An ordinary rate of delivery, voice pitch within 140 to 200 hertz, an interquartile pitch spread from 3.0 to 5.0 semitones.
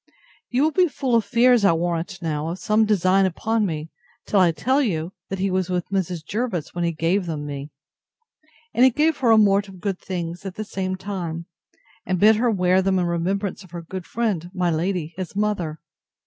No: fast, 210 wpm; medium, 185 Hz; average, 3.7 semitones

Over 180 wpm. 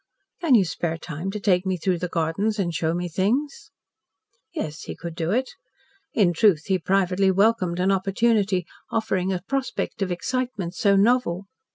No: average, 170 wpm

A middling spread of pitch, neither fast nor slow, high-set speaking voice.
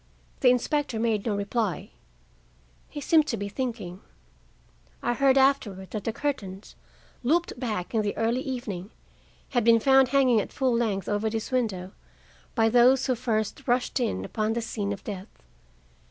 Yes: average, 3.7 semitones; average, 160 wpm; high, 230 Hz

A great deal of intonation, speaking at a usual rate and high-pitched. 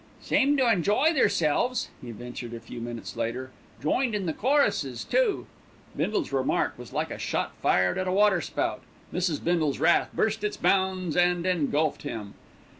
No: wide, 8.0 semitones; average, 160 wpm; medium, 175 Hz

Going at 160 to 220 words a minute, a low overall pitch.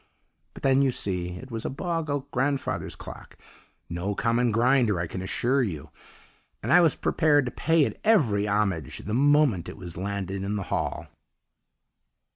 Yes: average, 170 wpm; low, 115 Hz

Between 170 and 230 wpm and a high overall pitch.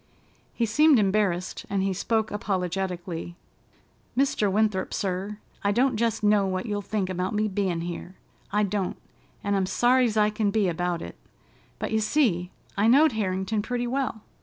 No: average, 160 wpm; high, 205 Hz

